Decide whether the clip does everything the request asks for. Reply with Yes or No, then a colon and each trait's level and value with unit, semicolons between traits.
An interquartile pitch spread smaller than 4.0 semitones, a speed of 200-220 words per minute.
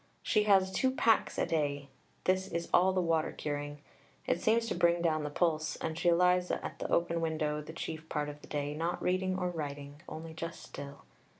Yes: average, 3.3 semitones; fast, 205 wpm